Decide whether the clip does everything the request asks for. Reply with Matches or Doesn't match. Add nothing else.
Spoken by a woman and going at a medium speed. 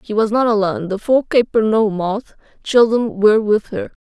Matches